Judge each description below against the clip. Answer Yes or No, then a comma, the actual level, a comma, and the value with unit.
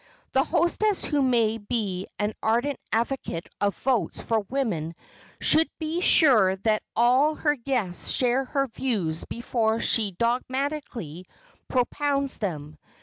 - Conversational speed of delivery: No, slow, 125 wpm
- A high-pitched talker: Yes, high, 240 Hz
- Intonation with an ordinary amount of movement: Yes, average, 5.0 semitones